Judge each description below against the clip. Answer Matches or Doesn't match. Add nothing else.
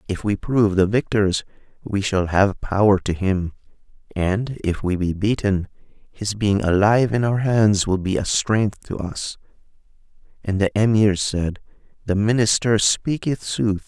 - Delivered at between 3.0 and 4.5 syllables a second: Matches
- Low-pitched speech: Matches